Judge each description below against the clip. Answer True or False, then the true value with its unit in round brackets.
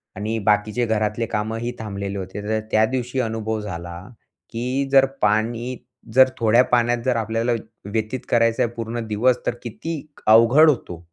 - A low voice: True (115 Hz)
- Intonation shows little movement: True (2.2 semitones)